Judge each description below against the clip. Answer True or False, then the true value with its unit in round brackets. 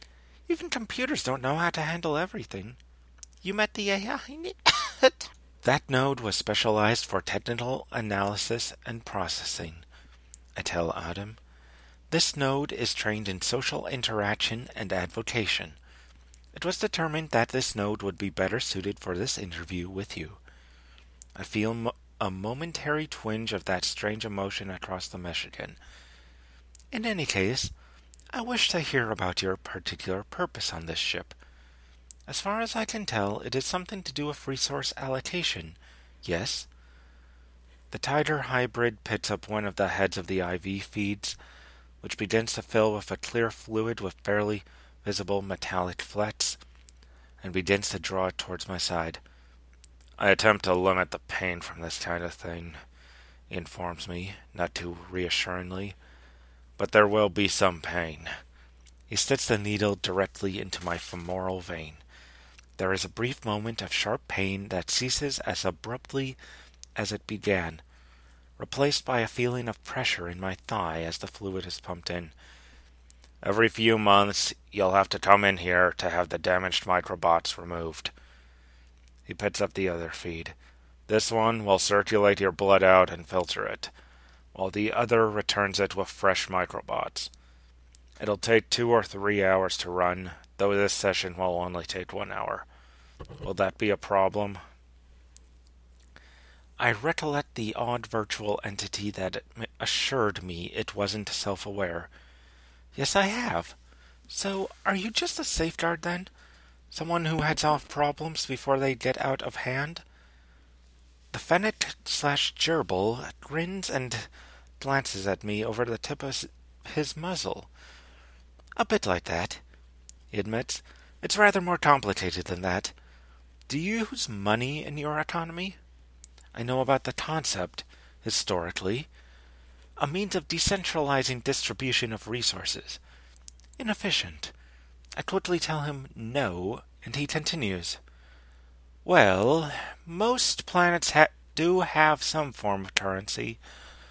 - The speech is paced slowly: False (145 wpm)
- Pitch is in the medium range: False (95 Hz)